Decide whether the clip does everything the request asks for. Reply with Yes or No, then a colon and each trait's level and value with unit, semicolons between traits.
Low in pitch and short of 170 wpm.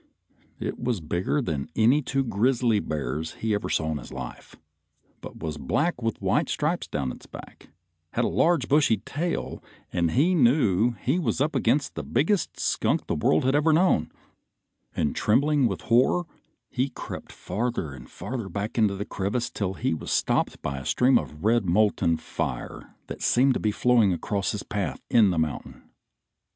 No: low, 110 Hz; average, 175 wpm